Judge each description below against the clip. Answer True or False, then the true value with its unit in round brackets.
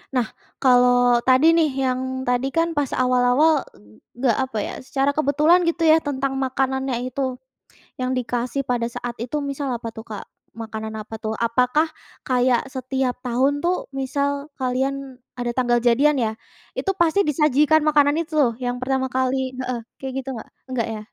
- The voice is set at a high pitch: True (260 Hz)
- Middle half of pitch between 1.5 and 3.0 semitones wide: True (2.5 semitones)